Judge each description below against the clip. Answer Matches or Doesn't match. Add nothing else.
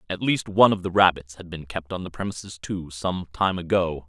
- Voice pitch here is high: Doesn't match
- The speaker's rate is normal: Doesn't match